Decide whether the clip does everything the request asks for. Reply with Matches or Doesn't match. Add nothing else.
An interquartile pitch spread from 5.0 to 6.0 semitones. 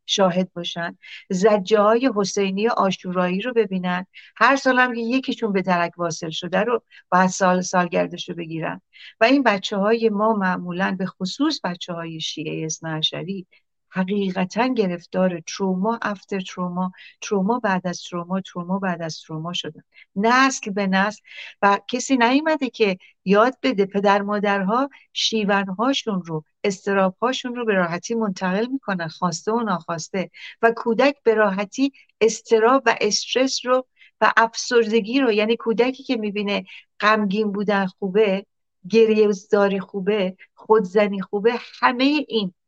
Doesn't match